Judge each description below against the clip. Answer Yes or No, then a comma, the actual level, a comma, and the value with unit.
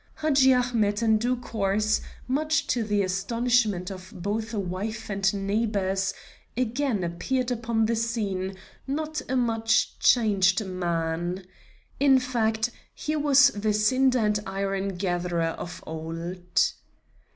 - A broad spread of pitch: No, average, 4.2 semitones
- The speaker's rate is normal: No, slow, 120 wpm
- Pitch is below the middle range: No, high, 215 Hz